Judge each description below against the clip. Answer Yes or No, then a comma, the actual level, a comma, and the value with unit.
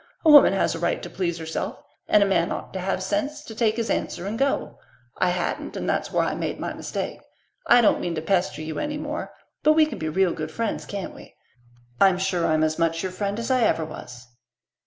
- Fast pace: Yes, fast, 235 wpm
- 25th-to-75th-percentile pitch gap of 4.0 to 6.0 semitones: Yes, wide, 5.6 semitones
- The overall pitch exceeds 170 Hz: Yes, high, 190 Hz